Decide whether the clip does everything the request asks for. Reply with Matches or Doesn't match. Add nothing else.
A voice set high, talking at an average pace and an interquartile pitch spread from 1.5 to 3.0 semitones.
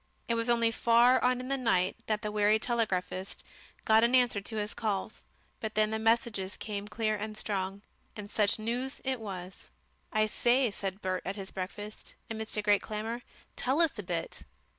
Matches